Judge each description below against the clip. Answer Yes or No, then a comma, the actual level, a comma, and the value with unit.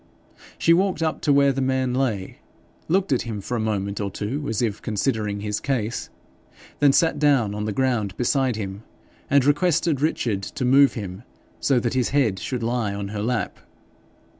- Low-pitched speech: Yes, low, 125 Hz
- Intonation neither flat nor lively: Yes, average, 5.0 semitones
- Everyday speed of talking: Yes, average, 185 wpm